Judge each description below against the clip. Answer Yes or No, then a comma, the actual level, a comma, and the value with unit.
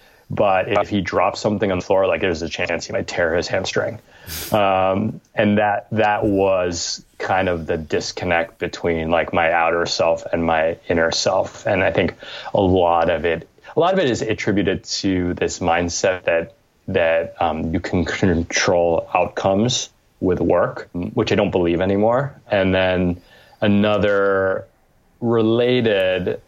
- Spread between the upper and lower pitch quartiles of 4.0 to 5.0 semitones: No, average, 3.3 semitones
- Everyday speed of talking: Yes, average, 155 wpm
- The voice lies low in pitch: Yes, very low, 95 Hz